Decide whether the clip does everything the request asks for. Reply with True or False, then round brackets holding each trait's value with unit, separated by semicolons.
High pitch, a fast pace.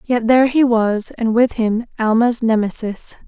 False (230 Hz; 145 wpm)